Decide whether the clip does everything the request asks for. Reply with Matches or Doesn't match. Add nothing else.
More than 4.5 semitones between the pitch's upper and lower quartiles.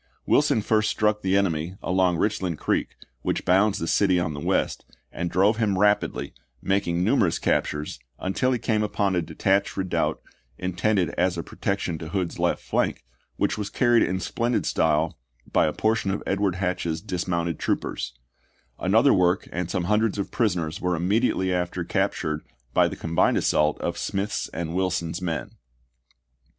Doesn't match